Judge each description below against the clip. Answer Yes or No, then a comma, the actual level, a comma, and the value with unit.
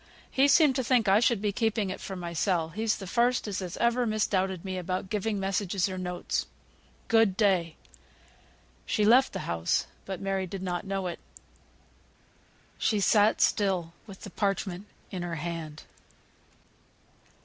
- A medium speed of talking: Yes, average, 155 wpm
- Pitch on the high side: Yes, high, 195 Hz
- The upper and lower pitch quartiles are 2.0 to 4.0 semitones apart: Yes, average, 3.0 semitones